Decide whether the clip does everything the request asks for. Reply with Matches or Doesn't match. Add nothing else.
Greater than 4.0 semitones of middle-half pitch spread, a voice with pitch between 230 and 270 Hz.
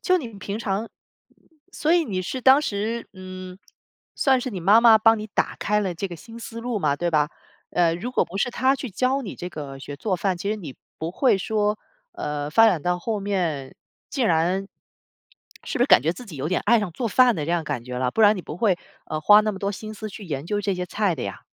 Doesn't match